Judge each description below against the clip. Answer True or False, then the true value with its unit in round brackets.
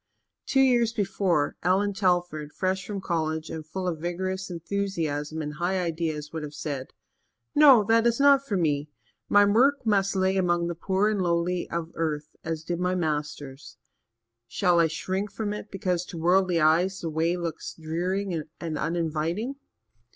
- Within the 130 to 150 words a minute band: False (165 wpm)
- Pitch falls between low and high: True (175 Hz)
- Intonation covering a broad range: False (3.5 semitones)